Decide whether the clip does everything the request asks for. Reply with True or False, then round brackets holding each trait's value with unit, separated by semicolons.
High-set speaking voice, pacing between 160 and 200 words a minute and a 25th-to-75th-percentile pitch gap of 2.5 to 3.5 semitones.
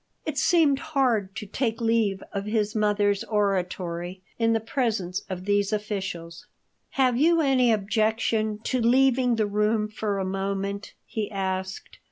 False (210 Hz; 145 wpm; 3.0 semitones)